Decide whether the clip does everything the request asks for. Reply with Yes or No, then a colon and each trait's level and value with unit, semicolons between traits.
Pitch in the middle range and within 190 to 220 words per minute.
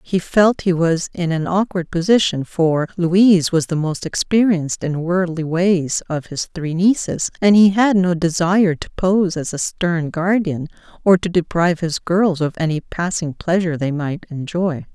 No: medium, 175 Hz; average, 175 wpm